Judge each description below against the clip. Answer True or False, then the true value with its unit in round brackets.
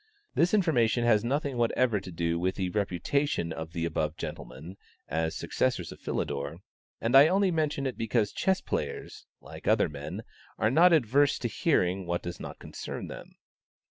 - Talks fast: False (170 wpm)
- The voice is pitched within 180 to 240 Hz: False (110 Hz)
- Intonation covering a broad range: True (8.5 semitones)